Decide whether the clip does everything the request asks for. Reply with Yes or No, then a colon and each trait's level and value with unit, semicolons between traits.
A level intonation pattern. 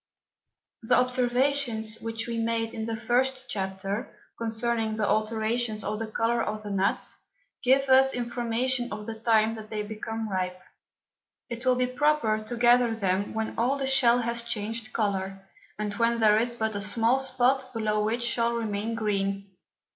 Yes: narrow, 2.1 semitones